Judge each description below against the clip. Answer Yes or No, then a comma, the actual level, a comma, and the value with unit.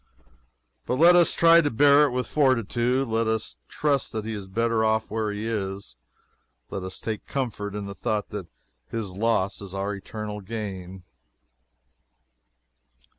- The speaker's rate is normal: Yes, average, 155 wpm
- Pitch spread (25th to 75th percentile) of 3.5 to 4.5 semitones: Yes, average, 3.8 semitones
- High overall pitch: No, low, 110 Hz